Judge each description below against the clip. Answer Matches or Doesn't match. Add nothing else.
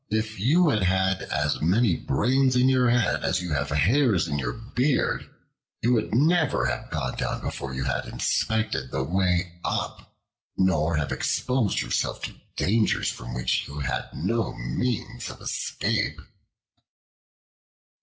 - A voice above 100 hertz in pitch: Doesn't match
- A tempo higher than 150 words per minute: Doesn't match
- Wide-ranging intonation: Matches